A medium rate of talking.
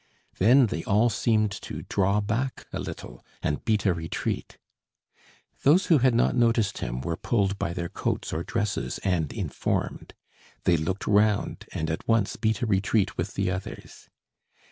Yes: average, 165 wpm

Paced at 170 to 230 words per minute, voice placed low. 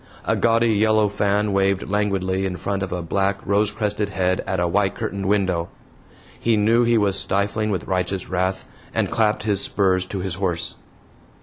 Yes: average, 180 wpm; low, 100 Hz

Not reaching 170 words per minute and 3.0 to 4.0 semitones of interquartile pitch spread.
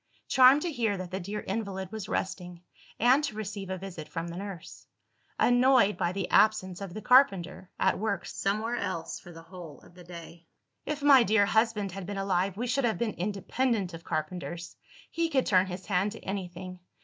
No: average, 195 wpm; average, 3.7 semitones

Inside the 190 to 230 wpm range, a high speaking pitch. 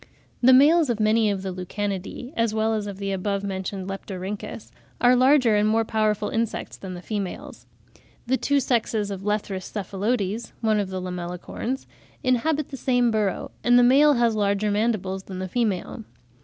No: average, 170 wpm; high, 215 Hz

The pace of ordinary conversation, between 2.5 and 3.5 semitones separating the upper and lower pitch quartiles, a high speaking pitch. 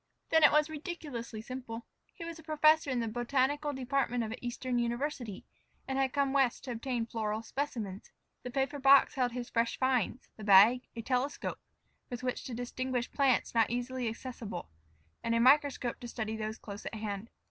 Yes: average, 180 wpm; average, 3.1 semitones; very high, 250 Hz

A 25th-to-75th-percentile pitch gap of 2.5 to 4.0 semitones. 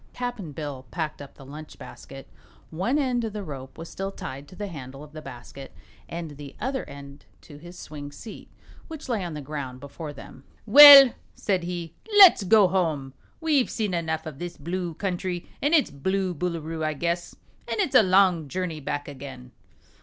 No: average, 5.3 semitones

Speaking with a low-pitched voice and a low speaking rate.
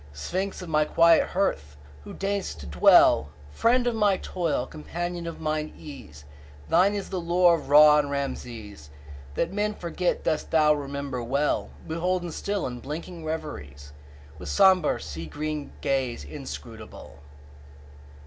No: medium, 150 Hz; slow, 125 wpm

